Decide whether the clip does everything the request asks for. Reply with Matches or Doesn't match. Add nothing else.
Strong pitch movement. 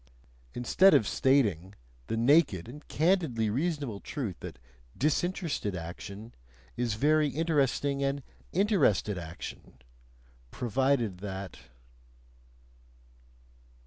Matches